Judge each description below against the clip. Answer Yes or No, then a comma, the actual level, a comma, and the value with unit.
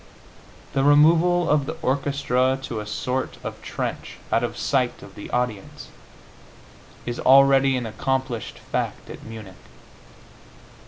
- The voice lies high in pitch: No, low, 130 Hz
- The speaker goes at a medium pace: No, slow, 125 wpm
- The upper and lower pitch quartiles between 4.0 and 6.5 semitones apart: No, average, 2.7 semitones